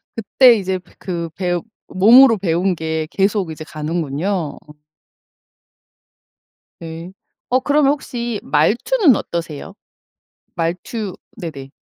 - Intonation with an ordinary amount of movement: No, wide, 5.7 semitones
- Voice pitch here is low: No, medium, 185 Hz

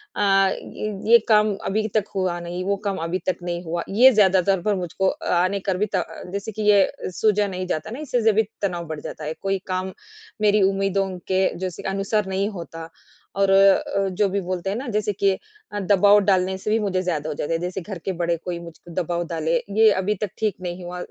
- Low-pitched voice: No, high, 195 Hz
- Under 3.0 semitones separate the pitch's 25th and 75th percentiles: Yes, narrow, 2.5 semitones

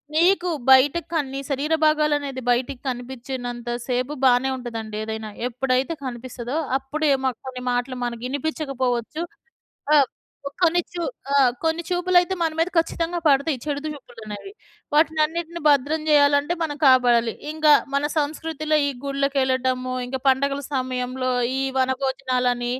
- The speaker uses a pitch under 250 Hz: No, very high, 270 Hz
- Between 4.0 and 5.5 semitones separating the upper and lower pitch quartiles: No, average, 3.5 semitones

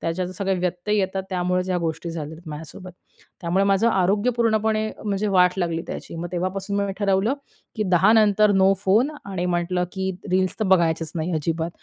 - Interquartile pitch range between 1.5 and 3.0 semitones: Yes, narrow, 2.6 semitones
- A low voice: No, medium, 185 Hz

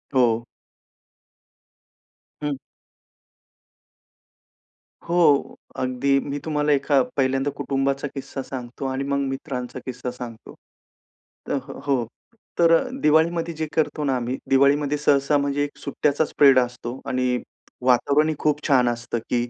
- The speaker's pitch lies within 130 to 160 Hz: Yes, medium, 140 Hz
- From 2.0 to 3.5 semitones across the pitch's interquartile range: Yes, narrow, 2.5 semitones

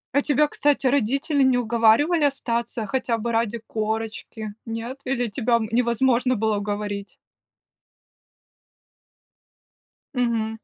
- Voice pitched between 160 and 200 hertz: No, high, 235 Hz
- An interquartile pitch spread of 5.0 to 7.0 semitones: No, average, 3.0 semitones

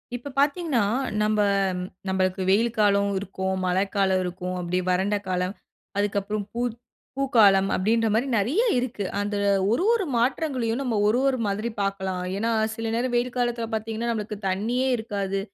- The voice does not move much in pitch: No, average, 3.6 semitones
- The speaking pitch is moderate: No, high, 215 Hz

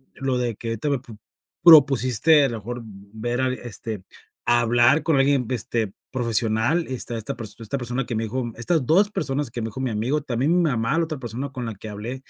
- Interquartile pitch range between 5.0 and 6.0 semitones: No, average, 3.4 semitones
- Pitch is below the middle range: Yes, low, 125 Hz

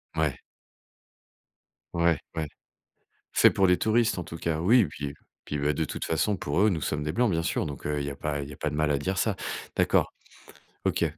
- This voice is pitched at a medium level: No, very low, 80 Hz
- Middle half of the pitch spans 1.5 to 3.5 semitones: No, average, 4.3 semitones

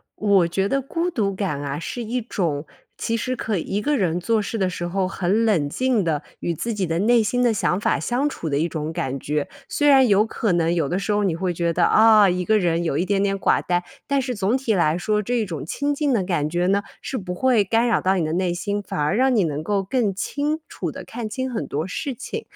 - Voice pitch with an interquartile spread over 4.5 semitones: Yes, average, 5.2 semitones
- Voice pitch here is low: No, high, 195 Hz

